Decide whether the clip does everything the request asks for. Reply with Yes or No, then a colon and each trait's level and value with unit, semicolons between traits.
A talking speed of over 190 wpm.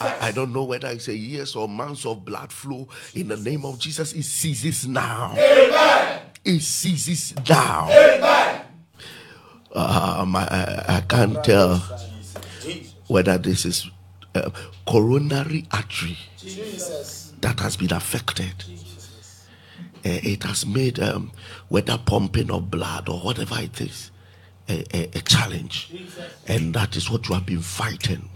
No: slow, 135 wpm